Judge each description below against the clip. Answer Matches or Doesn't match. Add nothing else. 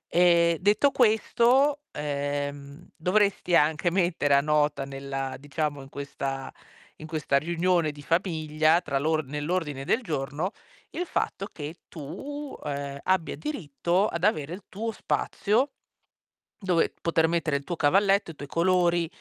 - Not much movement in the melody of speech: Doesn't match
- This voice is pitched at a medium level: Matches